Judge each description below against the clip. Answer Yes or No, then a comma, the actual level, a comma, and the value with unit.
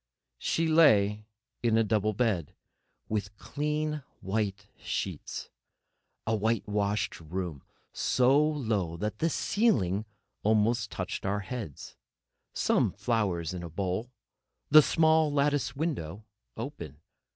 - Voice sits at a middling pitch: No, low, 110 Hz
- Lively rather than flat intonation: Yes, wide, 6.5 semitones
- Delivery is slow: Yes, slow, 115 wpm